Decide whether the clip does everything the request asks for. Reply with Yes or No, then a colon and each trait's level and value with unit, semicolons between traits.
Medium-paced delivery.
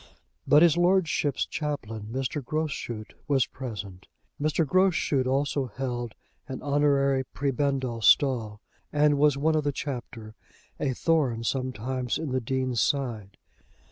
No: slow, 125 wpm